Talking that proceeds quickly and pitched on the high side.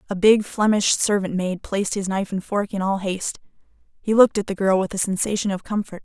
Yes: fast, 230 wpm; high, 195 Hz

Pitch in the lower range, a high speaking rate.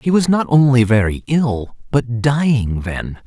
No: low, 125 Hz; average, 165 wpm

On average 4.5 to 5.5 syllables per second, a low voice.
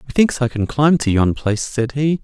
No: 5.9 syllables/s; low, 130 Hz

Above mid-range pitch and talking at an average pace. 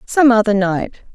Yes: high, 220 Hz; average, 155 wpm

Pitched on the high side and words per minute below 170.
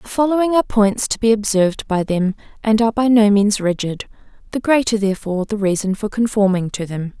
No: high, 210 Hz; average, 200 wpm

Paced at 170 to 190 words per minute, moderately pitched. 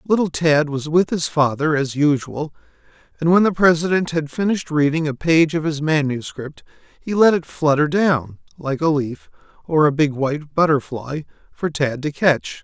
Yes: average, 175 wpm; medium, 155 Hz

